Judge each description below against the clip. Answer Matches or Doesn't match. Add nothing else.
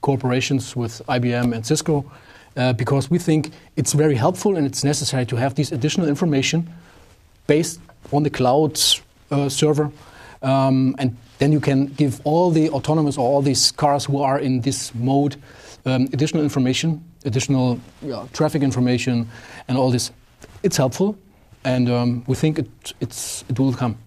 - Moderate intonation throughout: Matches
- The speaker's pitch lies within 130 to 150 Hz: Matches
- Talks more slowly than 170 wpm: Matches